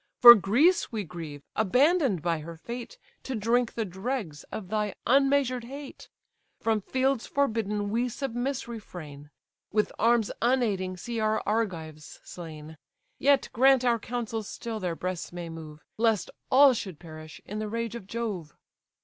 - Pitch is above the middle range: Yes, high, 220 Hz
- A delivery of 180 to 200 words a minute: No, average, 150 wpm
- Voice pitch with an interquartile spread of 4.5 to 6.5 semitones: Yes, wide, 5.4 semitones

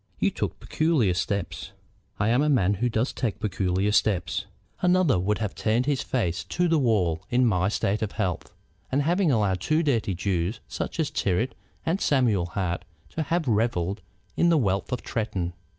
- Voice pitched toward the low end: Yes, low, 110 Hz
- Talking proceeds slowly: No, average, 180 wpm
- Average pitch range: No, wide, 6.6 semitones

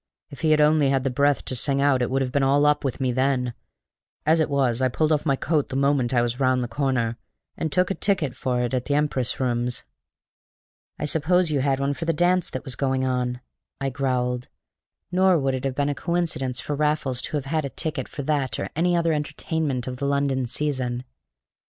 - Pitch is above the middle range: No, medium, 140 Hz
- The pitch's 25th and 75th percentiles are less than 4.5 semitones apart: Yes, average, 2.8 semitones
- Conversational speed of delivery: No, fast, 225 wpm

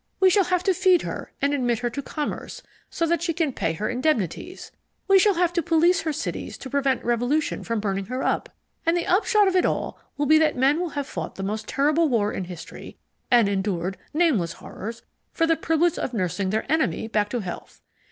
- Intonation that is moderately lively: No, wide, 7.6 semitones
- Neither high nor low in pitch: No, very high, 285 Hz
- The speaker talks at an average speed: No, fast, 215 wpm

